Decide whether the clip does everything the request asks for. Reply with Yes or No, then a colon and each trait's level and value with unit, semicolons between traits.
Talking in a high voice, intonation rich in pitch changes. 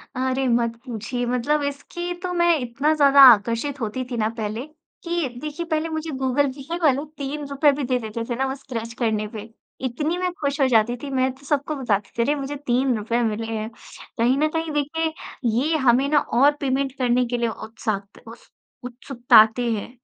No: very high, 260 Hz; average, 3.8 semitones